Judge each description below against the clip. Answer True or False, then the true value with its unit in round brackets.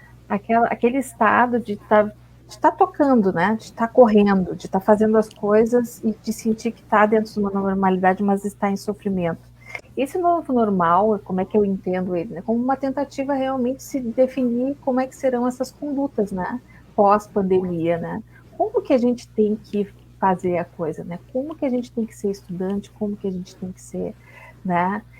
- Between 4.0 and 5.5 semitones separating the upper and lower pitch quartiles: True (4.7 semitones)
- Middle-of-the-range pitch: False (215 Hz)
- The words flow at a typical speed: False (200 wpm)